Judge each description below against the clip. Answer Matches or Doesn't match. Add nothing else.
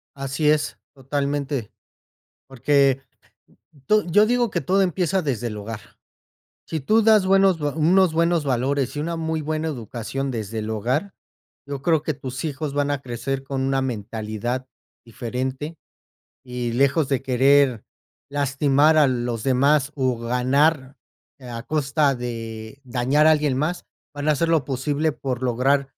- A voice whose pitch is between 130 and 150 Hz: Matches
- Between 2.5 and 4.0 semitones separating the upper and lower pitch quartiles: Matches